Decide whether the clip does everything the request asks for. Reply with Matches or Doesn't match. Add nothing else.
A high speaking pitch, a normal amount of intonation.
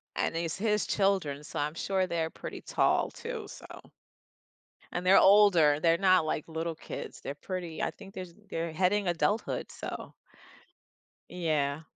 Doesn't match